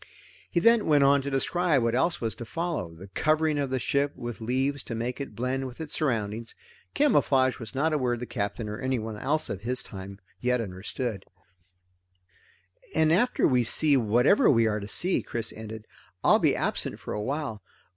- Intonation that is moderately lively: Yes, average, 4.7 semitones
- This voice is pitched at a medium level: No, low, 125 Hz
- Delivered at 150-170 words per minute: No, average, 185 wpm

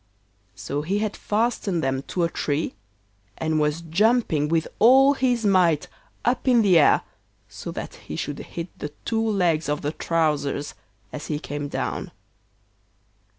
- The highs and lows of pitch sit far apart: Yes, wide, 6.4 semitones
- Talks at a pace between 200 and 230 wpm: No, average, 150 wpm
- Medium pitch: Yes, medium, 165 Hz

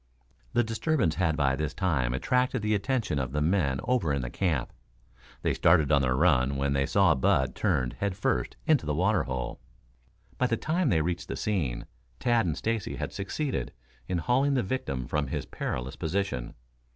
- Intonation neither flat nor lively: No, wide, 8.0 semitones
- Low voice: Yes, very low, 85 Hz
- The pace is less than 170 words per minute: No, average, 185 wpm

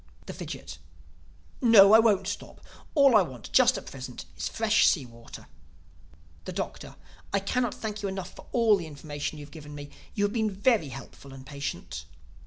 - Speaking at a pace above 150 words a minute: Yes, average, 185 wpm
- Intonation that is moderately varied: No, wide, 7.4 semitones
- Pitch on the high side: Yes, high, 195 Hz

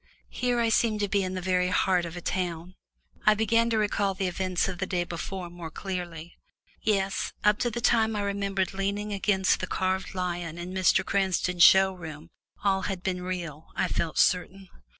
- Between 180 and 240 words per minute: Yes, average, 190 wpm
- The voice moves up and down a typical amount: No, narrow, 2.2 semitones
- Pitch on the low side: No, high, 190 Hz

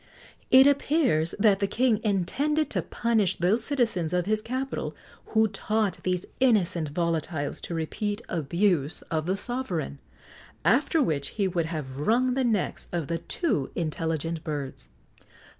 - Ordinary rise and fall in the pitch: No, wide, 6.3 semitones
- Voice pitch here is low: No, high, 190 Hz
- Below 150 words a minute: Yes, average, 140 wpm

